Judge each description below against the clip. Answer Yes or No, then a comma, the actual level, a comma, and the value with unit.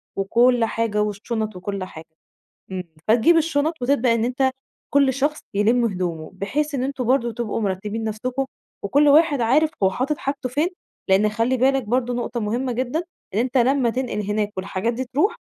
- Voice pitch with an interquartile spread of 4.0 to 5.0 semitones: Yes, average, 4.3 semitones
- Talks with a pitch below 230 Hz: No, high, 240 Hz